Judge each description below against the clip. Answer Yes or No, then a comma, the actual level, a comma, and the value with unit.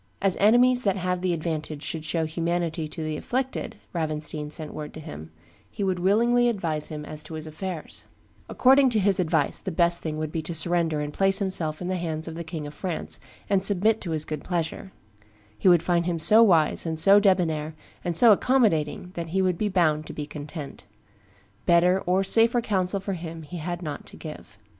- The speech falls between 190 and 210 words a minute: Yes, fast, 205 wpm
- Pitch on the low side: No, medium, 170 Hz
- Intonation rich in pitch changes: No, average, 3.6 semitones